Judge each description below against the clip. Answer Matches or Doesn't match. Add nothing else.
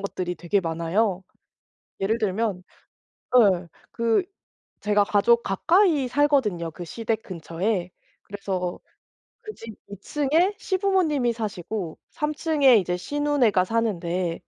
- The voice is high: Matches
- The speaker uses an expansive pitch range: Matches